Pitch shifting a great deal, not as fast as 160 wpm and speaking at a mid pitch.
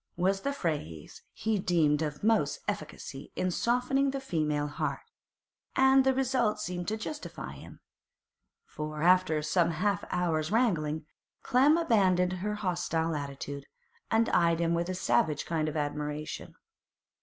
Yes: wide, 6.3 semitones; average, 140 wpm; medium, 175 Hz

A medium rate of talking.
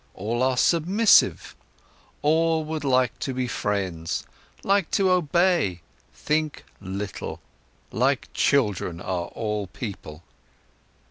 No: slow, 105 wpm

